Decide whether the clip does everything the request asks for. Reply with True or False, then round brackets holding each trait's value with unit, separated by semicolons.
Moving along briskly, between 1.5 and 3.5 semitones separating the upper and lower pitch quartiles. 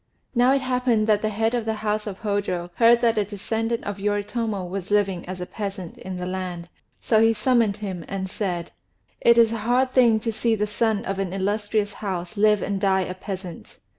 True (210 wpm; 2.9 semitones)